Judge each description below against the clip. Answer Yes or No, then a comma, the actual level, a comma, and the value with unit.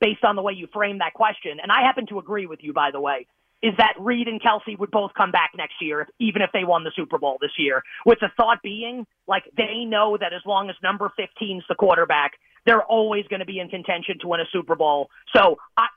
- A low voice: No, high, 205 Hz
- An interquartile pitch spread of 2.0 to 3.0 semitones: No, average, 3.8 semitones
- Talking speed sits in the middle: No, fast, 255 wpm